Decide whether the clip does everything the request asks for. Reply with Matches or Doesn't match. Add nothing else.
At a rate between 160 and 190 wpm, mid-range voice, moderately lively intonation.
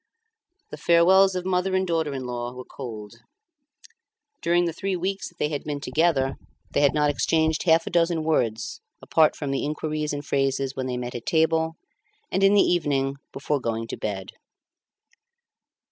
Matches